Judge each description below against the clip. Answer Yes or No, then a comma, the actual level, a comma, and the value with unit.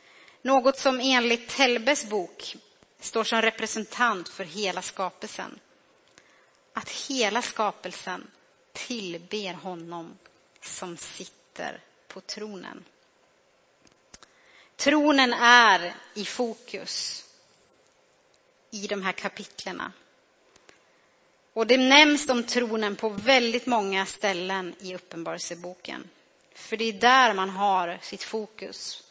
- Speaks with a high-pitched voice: Yes, high, 225 Hz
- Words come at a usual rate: No, slow, 95 wpm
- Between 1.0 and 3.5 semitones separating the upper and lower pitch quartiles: No, average, 5.3 semitones